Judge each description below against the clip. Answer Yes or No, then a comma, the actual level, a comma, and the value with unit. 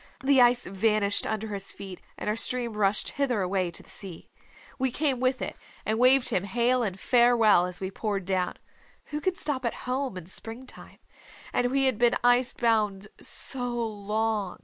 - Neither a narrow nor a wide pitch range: Yes, average, 4.1 semitones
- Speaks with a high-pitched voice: Yes, high, 225 Hz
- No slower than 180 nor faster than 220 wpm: Yes, average, 185 wpm